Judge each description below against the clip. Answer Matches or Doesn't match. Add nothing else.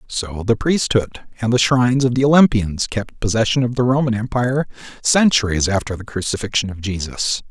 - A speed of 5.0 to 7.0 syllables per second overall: Matches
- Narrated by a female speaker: Doesn't match